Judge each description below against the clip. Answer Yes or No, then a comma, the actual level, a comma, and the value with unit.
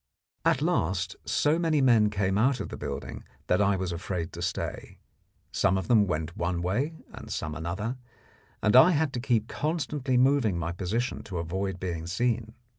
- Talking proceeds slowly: No, average, 180 wpm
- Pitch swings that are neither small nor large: No, wide, 6.2 semitones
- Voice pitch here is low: Yes, low, 105 Hz